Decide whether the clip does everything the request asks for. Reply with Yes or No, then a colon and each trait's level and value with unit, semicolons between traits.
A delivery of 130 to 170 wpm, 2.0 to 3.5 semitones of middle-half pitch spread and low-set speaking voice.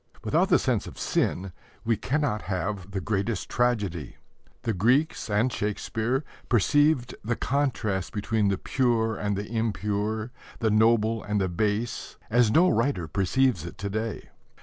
Yes: average, 150 wpm; average, 3.0 semitones; low, 110 Hz